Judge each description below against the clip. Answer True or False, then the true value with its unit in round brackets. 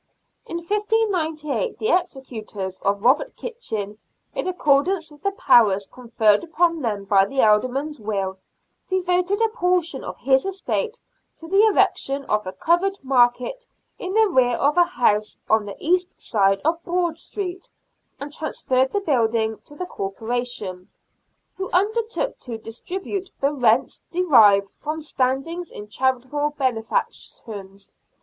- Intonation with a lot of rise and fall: True (8.5 semitones)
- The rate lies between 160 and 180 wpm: False (135 wpm)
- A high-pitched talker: True (280 Hz)